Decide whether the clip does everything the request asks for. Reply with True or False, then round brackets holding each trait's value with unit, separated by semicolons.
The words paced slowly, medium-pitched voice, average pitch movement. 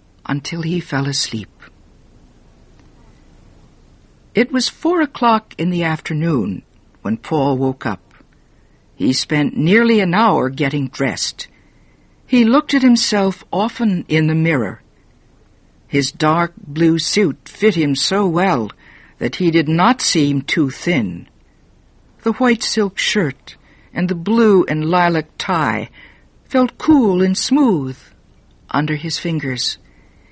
False (125 wpm; 165 Hz; 7.3 semitones)